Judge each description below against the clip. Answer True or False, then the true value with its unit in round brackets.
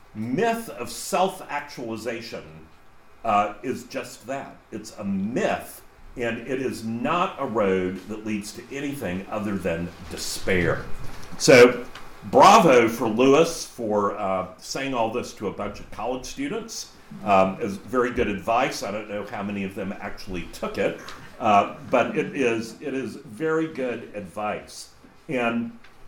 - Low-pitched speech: True (115 Hz)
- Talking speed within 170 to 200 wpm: False (140 wpm)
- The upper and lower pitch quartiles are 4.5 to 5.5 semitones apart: True (4.8 semitones)